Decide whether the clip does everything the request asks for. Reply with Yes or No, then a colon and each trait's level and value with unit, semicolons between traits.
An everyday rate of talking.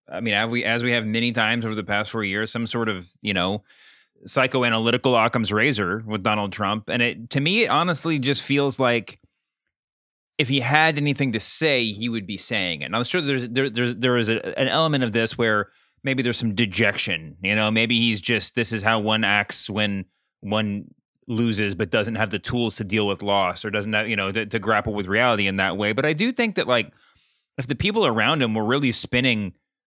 No: fast, 225 wpm